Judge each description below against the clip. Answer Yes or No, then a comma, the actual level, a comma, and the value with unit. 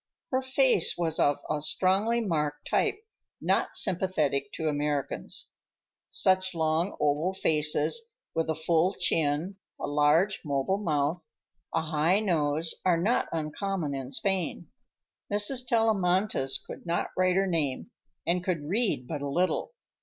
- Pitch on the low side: No, medium, 170 Hz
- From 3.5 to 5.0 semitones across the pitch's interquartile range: Yes, average, 4.4 semitones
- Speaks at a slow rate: Yes, slow, 130 wpm